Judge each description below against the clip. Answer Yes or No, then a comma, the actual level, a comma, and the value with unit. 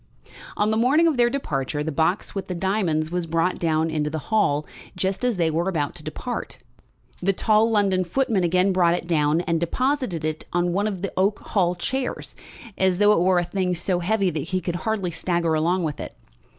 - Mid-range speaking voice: Yes, medium, 180 Hz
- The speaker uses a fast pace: Yes, fast, 210 wpm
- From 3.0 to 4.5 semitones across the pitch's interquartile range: Yes, average, 3.6 semitones